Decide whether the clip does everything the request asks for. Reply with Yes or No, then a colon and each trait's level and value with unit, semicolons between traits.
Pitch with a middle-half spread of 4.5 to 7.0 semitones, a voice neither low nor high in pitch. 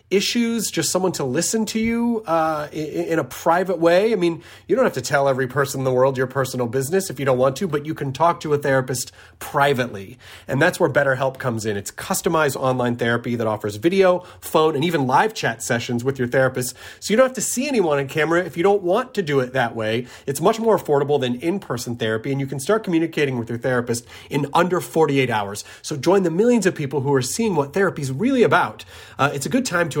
Yes: wide, 5.6 semitones; medium, 145 Hz